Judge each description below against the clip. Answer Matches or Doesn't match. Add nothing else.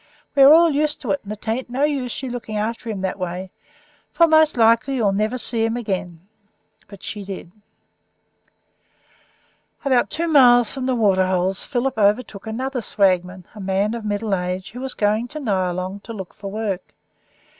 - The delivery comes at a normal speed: Matches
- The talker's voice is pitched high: Matches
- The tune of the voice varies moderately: Matches